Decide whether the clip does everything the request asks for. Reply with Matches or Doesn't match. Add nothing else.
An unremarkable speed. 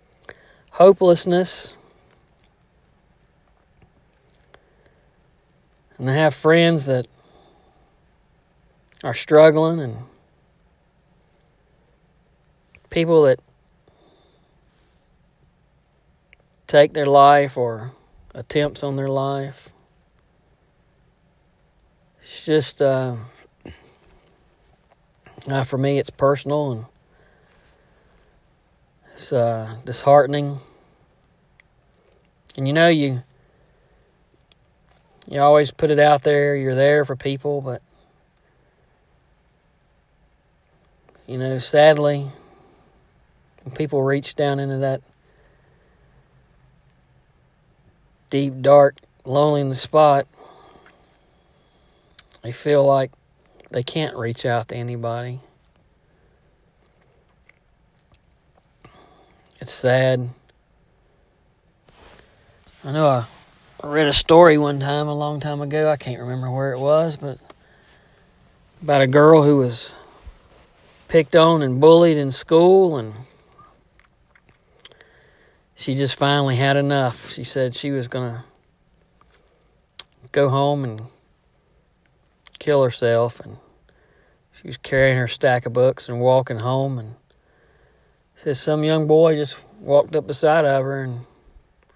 Doesn't match